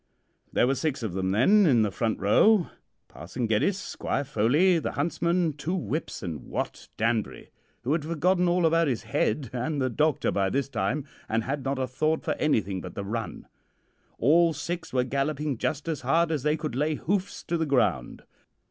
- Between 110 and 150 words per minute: No, average, 190 wpm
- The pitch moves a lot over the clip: Yes, wide, 6.0 semitones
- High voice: No, medium, 140 Hz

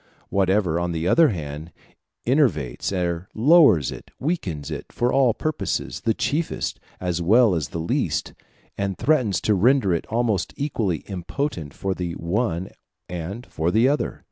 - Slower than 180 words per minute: Yes, average, 150 wpm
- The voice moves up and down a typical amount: No, wide, 6.5 semitones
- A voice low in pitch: Yes, very low, 95 Hz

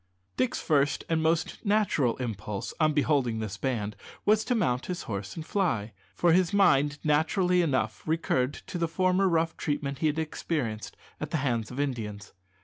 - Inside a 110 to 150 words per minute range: No, average, 170 wpm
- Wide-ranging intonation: Yes, wide, 5.7 semitones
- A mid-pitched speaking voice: Yes, medium, 145 Hz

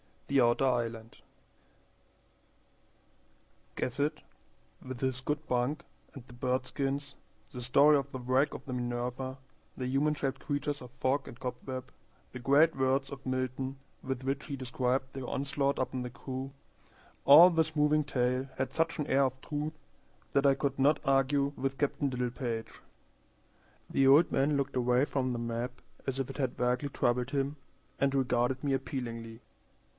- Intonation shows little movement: Yes, narrow, 1.9 semitones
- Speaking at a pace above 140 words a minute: Yes, average, 160 wpm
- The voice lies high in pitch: No, low, 135 Hz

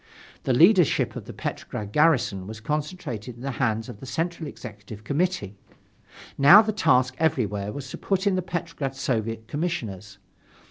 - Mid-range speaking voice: No, low, 130 Hz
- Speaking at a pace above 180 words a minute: No, average, 155 wpm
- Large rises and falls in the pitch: Yes, wide, 7.2 semitones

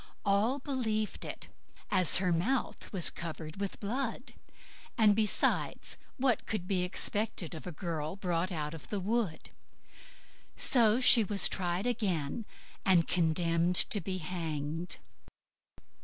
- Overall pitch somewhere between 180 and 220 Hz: Yes, medium, 185 Hz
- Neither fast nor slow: No, slow, 125 wpm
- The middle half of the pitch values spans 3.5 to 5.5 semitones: Yes, average, 4.4 semitones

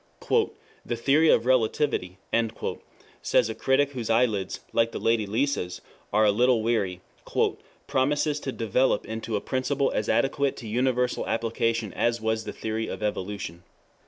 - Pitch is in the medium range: No, low, 115 Hz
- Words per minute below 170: Yes, average, 150 wpm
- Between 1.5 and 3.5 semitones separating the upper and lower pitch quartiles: Yes, average, 3.1 semitones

